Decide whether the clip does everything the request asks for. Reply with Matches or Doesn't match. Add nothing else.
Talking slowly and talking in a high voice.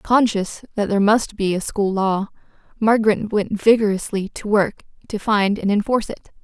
Doesn't match